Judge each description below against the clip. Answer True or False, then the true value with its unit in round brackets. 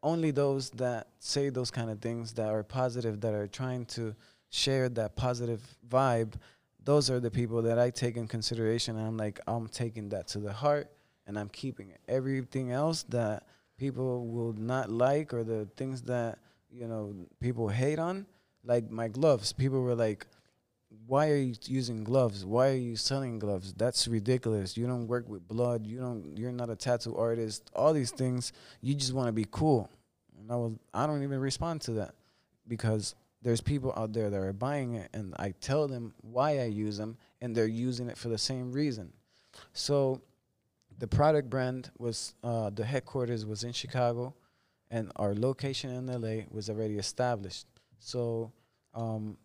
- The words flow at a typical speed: True (185 wpm)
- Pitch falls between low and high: False (120 Hz)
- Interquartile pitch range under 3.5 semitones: True (2.8 semitones)